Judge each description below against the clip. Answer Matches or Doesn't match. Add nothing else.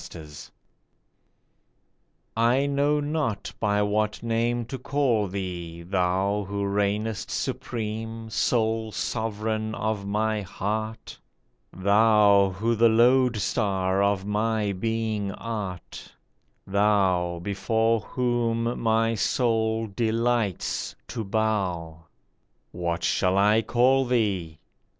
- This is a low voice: Matches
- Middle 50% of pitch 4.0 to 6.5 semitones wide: Doesn't match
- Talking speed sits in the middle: Doesn't match